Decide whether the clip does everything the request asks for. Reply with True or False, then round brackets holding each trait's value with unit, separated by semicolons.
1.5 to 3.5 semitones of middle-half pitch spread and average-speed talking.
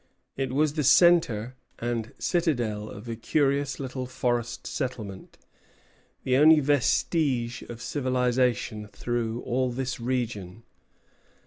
False (2.9 semitones; 110 wpm)